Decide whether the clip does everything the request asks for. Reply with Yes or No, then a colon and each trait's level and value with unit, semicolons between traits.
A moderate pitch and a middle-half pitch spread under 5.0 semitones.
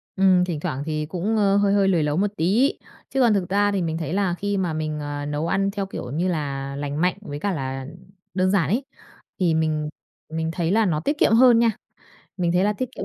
Yes: medium, 180 Hz; average, 4.6 semitones